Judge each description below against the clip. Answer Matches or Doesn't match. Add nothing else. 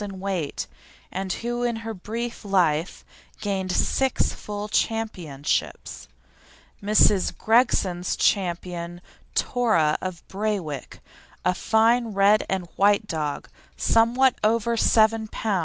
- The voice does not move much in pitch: Doesn't match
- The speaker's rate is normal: Doesn't match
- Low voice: Doesn't match